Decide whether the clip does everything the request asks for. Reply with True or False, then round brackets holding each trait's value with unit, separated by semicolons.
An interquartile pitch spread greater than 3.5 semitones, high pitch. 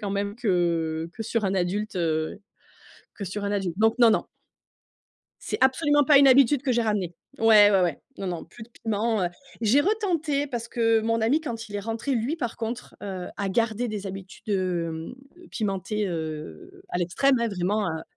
True (4.2 semitones; 215 Hz)